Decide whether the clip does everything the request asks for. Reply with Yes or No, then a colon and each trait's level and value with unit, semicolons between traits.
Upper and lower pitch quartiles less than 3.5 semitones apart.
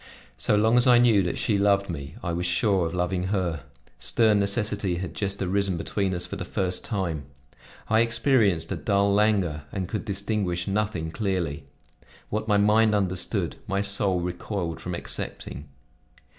Yes: average, 3.0 semitones